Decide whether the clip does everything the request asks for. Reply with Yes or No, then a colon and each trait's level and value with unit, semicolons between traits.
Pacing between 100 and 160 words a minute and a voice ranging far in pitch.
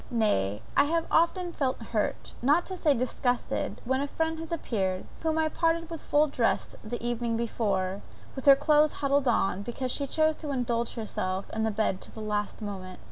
No: average, 190 wpm; wide, 6.0 semitones